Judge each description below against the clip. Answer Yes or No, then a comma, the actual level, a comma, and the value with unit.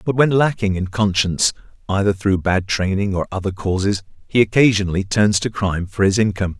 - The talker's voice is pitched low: Yes, low, 100 Hz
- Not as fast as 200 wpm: Yes, average, 180 wpm